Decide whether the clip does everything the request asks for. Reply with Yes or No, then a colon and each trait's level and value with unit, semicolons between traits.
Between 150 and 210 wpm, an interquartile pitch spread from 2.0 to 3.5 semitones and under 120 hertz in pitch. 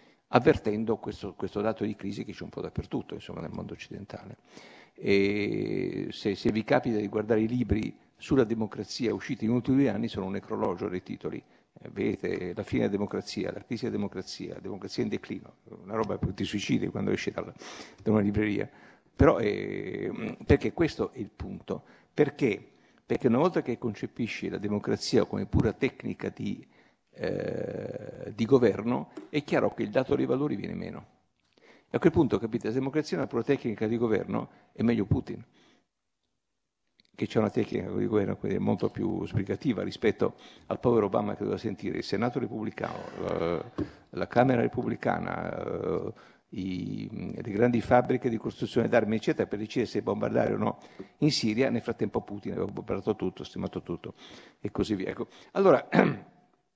Yes: fast, 170 wpm; average, 2.7 semitones; low, 110 Hz